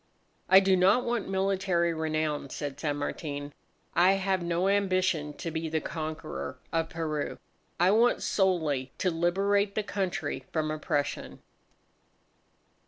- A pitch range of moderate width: Yes, average, 3.7 semitones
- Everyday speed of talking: No, slow, 130 wpm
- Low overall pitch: No, medium, 170 Hz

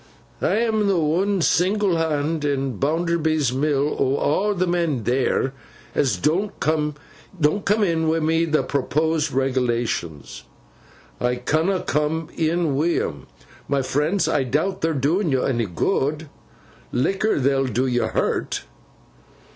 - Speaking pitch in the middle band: Yes, medium, 155 Hz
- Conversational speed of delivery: No, slow, 125 wpm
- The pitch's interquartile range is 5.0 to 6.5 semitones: No, average, 4.0 semitones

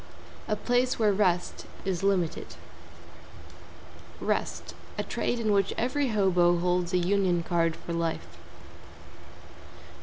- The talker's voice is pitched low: No, medium, 185 Hz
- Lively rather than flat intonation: No, average, 3.4 semitones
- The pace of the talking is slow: Yes, slow, 115 wpm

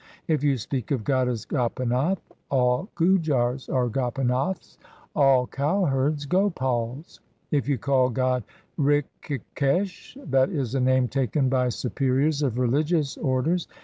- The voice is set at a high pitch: No, low, 135 Hz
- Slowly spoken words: Yes, slow, 130 wpm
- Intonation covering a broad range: No, average, 2.8 semitones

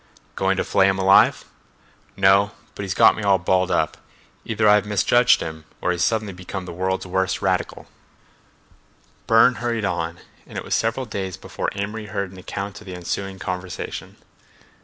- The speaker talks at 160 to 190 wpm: Yes, average, 165 wpm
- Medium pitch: No, very low, 95 Hz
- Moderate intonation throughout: No, narrow, 2.1 semitones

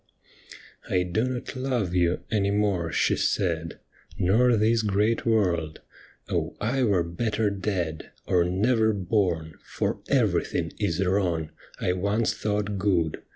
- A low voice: Yes, low, 100 Hz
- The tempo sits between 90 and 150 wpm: Yes, average, 140 wpm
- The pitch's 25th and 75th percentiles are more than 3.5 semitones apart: Yes, average, 3.9 semitones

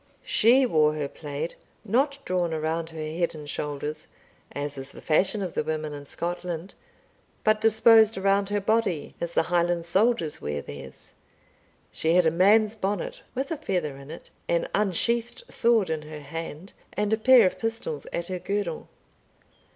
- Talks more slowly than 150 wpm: No, average, 165 wpm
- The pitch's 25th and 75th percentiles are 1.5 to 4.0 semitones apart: No, wide, 5.6 semitones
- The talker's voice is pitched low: No, medium, 175 Hz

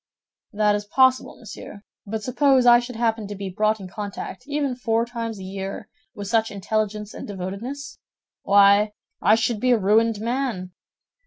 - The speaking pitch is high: Yes, high, 220 Hz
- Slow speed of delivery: No, average, 160 wpm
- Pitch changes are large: No, average, 3.1 semitones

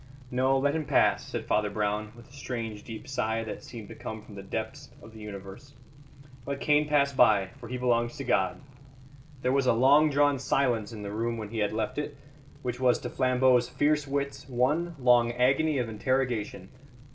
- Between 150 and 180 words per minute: No, average, 195 wpm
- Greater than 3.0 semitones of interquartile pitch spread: Yes, average, 4.0 semitones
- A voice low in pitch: Yes, low, 125 Hz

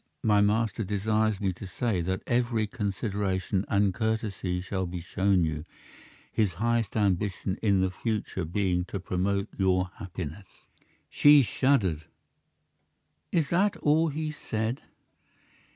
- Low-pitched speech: Yes, low, 100 Hz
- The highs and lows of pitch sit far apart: No, average, 3.2 semitones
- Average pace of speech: No, slow, 125 wpm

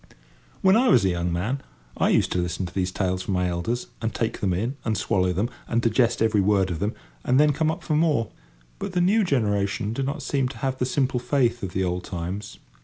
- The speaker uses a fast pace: Yes, fast, 240 wpm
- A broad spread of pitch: Yes, wide, 6.3 semitones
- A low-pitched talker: Yes, low, 110 Hz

